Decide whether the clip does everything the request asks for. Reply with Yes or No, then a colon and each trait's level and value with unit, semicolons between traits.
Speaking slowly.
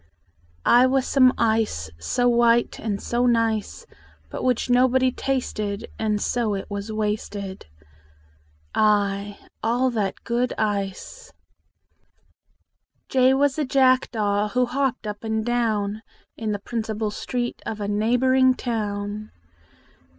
Yes: slow, 120 wpm